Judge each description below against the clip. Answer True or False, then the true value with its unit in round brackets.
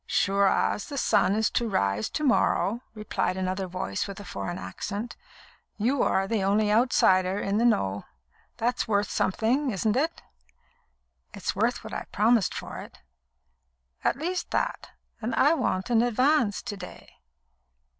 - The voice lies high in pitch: True (210 Hz)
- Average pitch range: True (4.2 semitones)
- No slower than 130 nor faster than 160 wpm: True (155 wpm)